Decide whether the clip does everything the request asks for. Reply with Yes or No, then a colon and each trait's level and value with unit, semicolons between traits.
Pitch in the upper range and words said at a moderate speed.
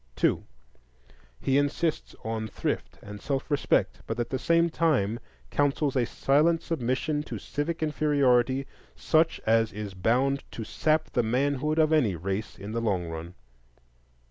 No: low, 135 Hz; average, 145 wpm